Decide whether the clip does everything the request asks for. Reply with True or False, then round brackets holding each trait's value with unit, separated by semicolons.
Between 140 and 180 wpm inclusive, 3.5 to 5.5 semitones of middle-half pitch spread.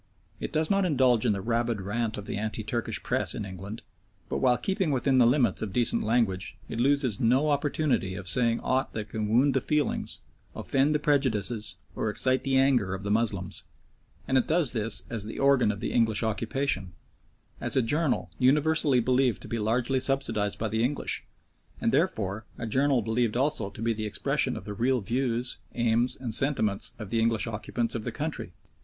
False (195 wpm; 3.8 semitones)